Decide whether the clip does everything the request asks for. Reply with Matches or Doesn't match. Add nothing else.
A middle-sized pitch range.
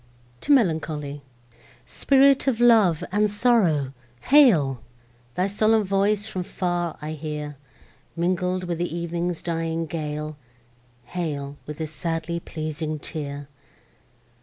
Matches